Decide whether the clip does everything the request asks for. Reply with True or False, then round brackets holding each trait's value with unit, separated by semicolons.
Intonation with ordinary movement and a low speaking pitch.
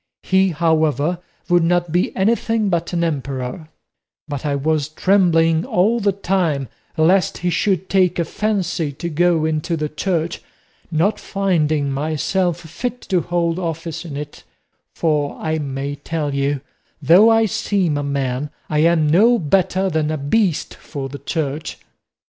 False (3.6 semitones; 165 Hz)